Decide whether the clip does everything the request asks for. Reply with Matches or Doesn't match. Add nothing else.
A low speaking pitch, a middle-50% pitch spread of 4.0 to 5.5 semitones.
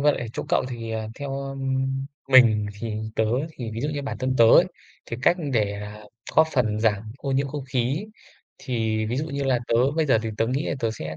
Doesn't match